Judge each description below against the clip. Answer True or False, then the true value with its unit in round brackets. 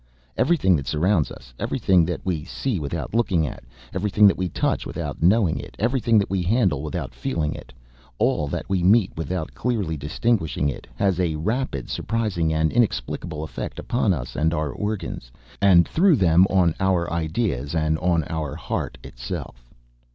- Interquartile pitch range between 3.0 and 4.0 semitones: False (4.9 semitones)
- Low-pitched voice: True (85 Hz)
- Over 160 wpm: True (175 wpm)